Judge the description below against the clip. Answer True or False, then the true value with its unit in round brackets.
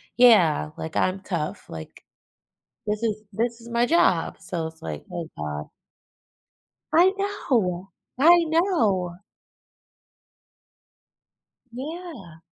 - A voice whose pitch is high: True (215 Hz)